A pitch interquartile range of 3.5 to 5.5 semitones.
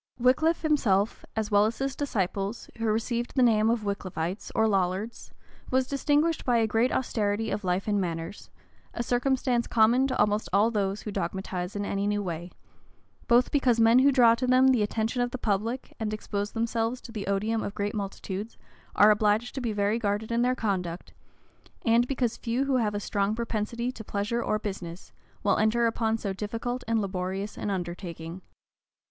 No: average, 3.0 semitones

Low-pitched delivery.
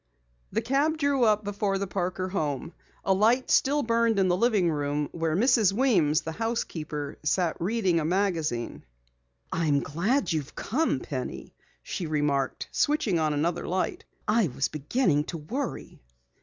No: medium, 185 Hz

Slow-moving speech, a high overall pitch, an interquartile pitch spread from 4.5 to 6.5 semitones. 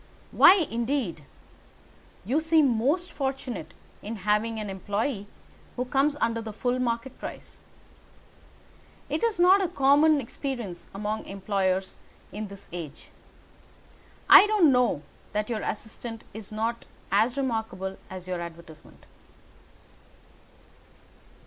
Yes: slow, 115 wpm; high, 230 Hz; wide, 5.5 semitones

